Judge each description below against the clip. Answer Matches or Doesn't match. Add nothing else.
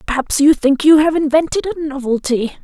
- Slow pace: Doesn't match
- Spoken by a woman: Matches